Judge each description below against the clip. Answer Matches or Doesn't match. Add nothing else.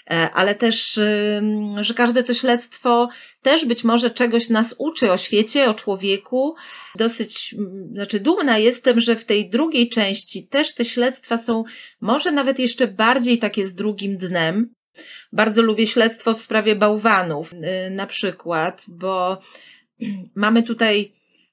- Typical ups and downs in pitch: Matches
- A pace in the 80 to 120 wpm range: Doesn't match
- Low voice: Doesn't match